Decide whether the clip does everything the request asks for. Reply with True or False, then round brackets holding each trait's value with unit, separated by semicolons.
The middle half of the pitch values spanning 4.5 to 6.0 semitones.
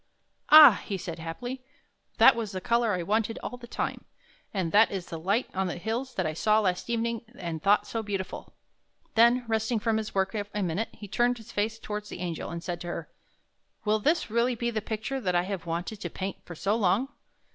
False (3.9 semitones)